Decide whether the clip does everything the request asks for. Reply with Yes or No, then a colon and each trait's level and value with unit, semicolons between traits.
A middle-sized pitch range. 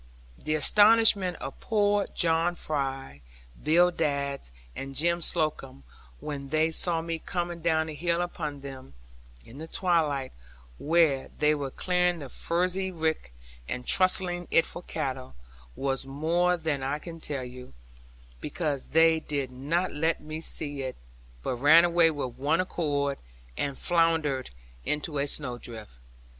Yes: average, 3.8 semitones